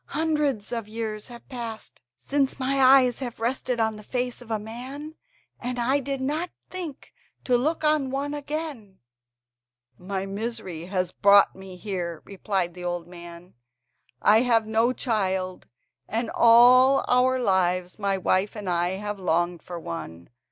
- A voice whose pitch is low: No, high, 225 Hz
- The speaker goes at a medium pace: Yes, average, 150 wpm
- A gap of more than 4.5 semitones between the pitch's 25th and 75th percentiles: Yes, wide, 5.5 semitones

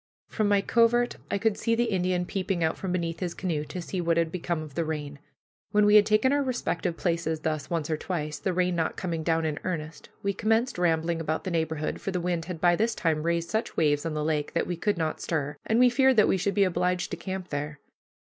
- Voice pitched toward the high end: No, medium, 175 Hz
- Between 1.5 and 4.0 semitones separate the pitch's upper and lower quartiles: Yes, average, 3.7 semitones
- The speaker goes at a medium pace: No, fast, 245 wpm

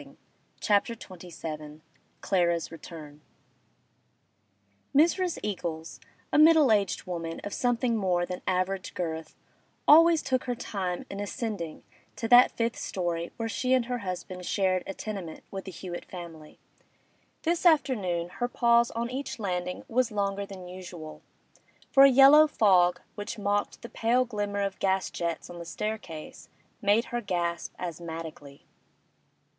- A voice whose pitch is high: Yes, high, 195 Hz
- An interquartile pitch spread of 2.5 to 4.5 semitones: No, average, 5.3 semitones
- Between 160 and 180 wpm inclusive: No, average, 140 wpm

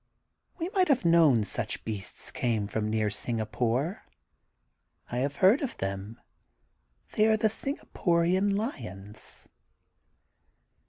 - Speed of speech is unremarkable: No, slow, 110 wpm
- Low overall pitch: Yes, low, 130 Hz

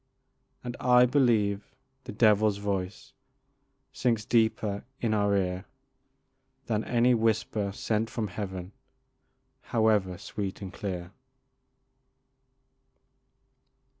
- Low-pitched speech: Yes, low, 105 Hz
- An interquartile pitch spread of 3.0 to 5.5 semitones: No, narrow, 2.4 semitones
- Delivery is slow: Yes, slow, 90 wpm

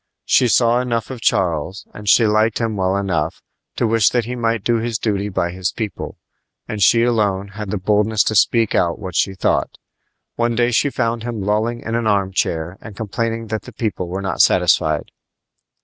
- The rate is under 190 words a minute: No, average, 195 wpm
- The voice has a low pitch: Yes, low, 110 Hz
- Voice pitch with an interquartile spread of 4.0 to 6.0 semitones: No, average, 3.2 semitones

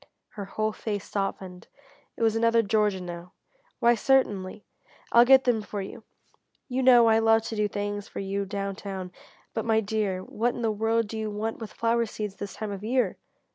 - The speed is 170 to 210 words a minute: Yes, average, 195 wpm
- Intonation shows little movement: Yes, narrow, 2.3 semitones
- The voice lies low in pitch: No, high, 215 Hz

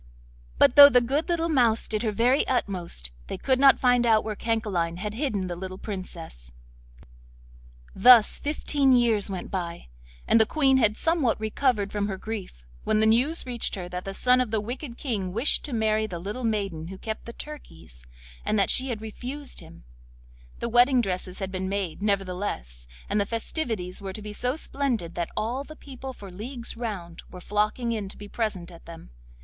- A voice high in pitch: Yes, high, 215 Hz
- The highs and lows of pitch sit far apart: No, average, 4.8 semitones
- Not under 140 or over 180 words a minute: No, average, 190 wpm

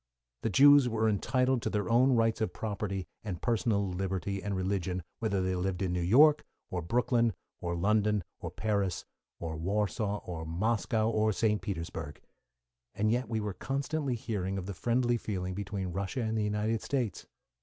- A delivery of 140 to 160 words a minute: No, average, 170 wpm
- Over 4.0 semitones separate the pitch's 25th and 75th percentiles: No, average, 3.5 semitones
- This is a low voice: Yes, low, 105 Hz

